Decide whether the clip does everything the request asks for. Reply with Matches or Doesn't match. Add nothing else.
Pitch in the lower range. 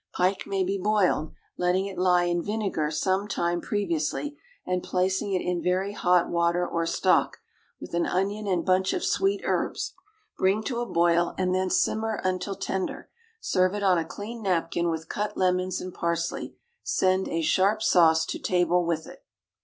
Doesn't match